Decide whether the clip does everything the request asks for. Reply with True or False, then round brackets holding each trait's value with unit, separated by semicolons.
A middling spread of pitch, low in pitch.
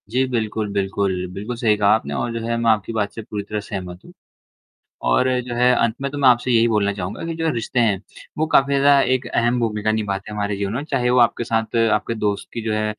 True (3.0 semitones; 110 Hz)